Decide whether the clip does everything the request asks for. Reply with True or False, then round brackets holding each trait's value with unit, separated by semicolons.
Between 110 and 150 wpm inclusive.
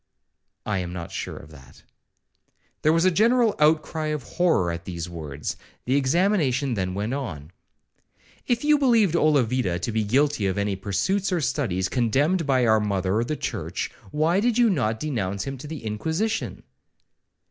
False (165 wpm)